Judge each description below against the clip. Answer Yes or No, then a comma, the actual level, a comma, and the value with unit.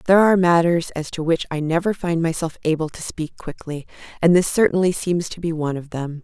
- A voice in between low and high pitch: Yes, medium, 165 Hz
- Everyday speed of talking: No, fast, 220 wpm